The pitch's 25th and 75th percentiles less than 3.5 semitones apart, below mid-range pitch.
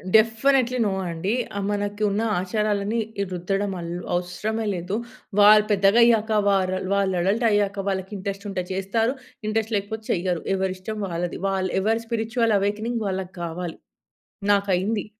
No: narrow, 2.6 semitones; high, 200 Hz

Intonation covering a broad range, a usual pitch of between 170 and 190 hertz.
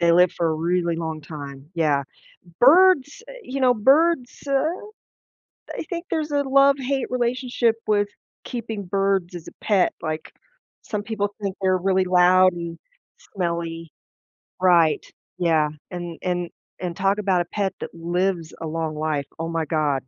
Yes: wide, 6.0 semitones; medium, 185 Hz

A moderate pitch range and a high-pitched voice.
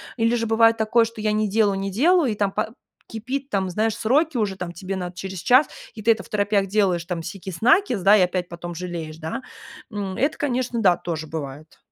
Yes: average, 4.2 semitones; high, 205 Hz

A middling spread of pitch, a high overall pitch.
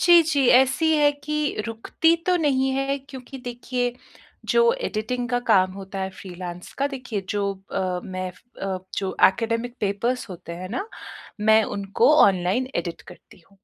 No: wide, 5.9 semitones; high, 235 Hz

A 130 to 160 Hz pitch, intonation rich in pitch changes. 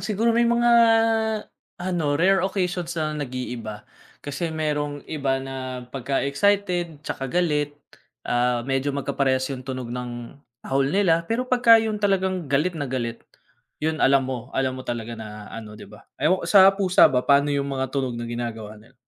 Yes: medium, 140 Hz; wide, 6.0 semitones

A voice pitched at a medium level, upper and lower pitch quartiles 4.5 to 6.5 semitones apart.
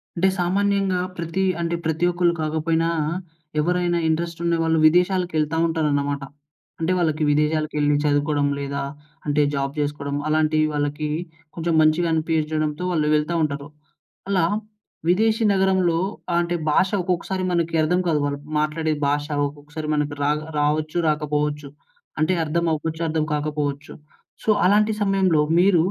No: medium, 155 Hz; narrow, 2.6 semitones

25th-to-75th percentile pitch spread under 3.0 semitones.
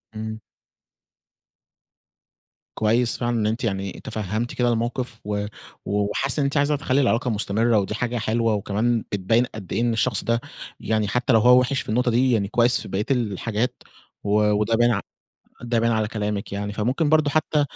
Yes: narrow, 2.6 semitones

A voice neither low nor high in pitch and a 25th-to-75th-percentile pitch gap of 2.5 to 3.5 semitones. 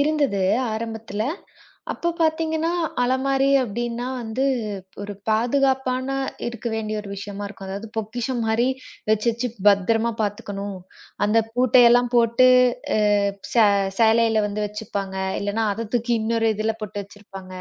No: high, 225 Hz; average, 3.1 semitones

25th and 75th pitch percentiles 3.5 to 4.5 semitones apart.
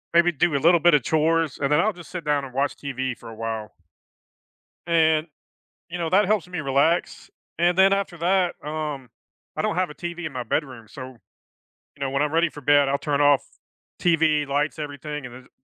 Yes: average, 3.8 semitones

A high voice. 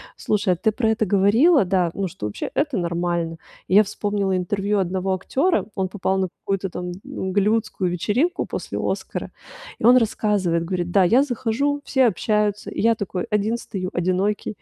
Yes: high, 200 Hz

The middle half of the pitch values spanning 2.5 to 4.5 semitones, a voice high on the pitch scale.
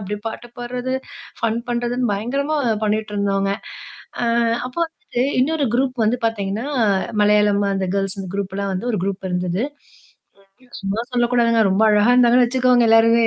Yes: average, 3.5 semitones; high, 225 Hz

